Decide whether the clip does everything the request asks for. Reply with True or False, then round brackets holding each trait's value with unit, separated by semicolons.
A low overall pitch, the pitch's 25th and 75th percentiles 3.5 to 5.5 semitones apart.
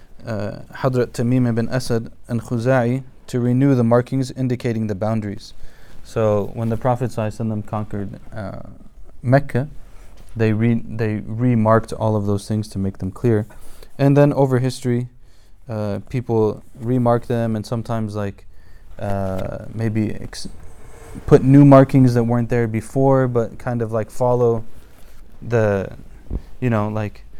False (115 Hz; 2.8 semitones)